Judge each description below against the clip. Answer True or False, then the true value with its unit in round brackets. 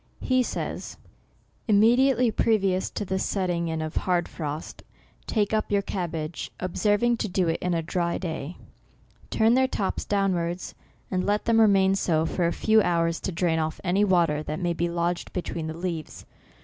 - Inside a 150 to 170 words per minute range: False (190 wpm)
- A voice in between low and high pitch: True (180 Hz)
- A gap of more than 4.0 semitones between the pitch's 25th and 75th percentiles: False (3.6 semitones)